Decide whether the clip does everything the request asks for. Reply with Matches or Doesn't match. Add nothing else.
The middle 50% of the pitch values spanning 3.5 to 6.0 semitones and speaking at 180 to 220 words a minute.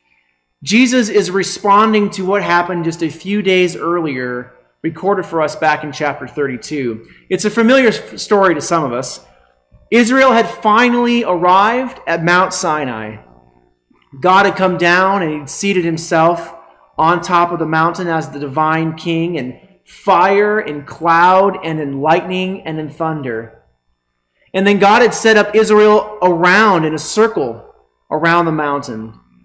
Doesn't match